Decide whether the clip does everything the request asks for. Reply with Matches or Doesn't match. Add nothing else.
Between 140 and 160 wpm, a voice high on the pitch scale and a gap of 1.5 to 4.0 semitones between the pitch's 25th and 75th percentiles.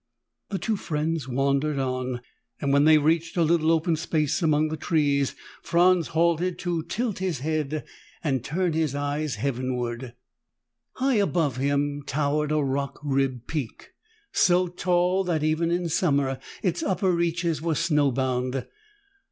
Doesn't match